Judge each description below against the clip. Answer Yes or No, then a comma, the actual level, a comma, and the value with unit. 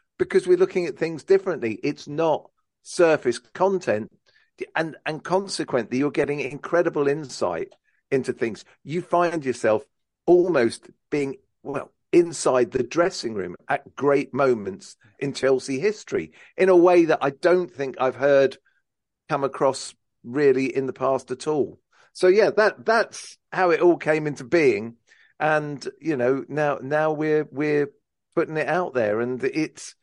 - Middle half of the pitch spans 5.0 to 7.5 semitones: Yes, wide, 5.4 semitones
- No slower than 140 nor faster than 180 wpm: Yes, average, 150 wpm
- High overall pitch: No, medium, 155 Hz